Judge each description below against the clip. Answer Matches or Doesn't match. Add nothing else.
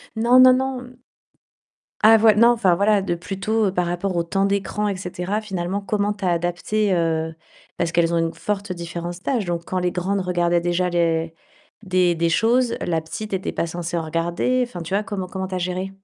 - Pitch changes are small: Doesn't match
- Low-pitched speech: Doesn't match